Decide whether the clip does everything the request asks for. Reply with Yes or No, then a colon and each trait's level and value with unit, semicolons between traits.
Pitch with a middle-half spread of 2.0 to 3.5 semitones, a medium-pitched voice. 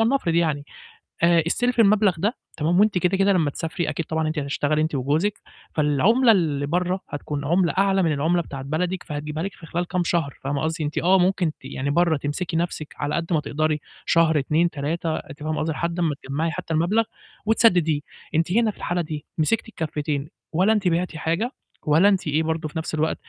Yes: average, 3.1 semitones; medium, 165 Hz